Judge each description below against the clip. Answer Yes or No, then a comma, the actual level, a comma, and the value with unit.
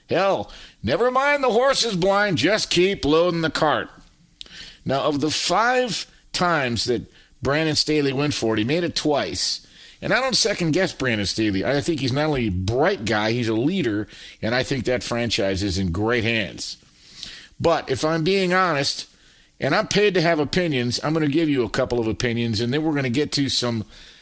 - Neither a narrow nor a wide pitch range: No, wide, 6.5 semitones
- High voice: No, medium, 140 Hz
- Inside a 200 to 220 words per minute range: Yes, fast, 205 wpm